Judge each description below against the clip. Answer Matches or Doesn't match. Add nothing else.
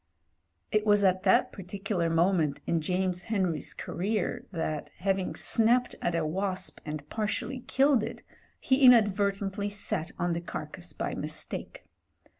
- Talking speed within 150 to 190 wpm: Doesn't match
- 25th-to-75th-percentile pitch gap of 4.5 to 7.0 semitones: Doesn't match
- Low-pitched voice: Doesn't match